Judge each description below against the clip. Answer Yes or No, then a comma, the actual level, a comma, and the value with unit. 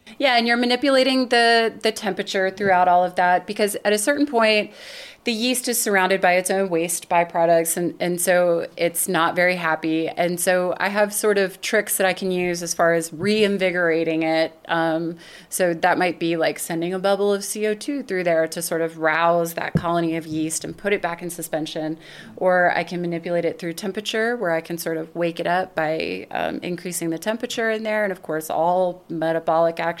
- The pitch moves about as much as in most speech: Yes, average, 3.6 semitones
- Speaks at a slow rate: No, fast, 205 wpm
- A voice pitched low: No, medium, 180 Hz